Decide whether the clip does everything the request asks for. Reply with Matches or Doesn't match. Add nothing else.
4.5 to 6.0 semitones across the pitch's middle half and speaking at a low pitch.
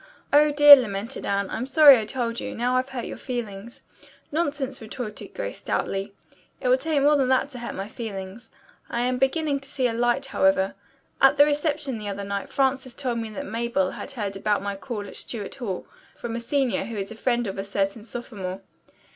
Doesn't match